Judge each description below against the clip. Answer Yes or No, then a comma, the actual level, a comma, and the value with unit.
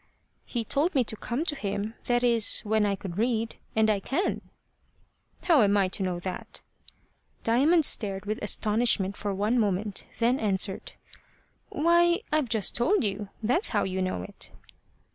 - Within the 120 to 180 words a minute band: Yes, average, 160 wpm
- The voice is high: Yes, high, 220 Hz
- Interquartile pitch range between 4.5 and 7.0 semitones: No, average, 3.9 semitones